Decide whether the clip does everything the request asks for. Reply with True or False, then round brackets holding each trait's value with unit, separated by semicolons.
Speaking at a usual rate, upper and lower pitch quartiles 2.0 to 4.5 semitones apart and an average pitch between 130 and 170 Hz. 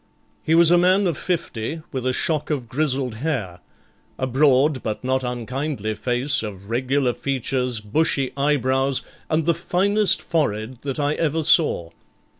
True (150 wpm; 4.1 semitones; 135 Hz)